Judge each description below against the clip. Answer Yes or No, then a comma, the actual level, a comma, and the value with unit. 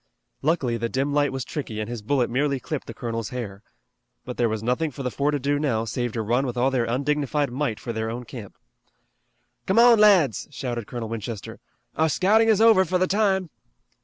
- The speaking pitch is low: Yes, low, 130 Hz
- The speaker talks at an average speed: No, fast, 210 wpm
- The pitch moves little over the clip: No, average, 4.3 semitones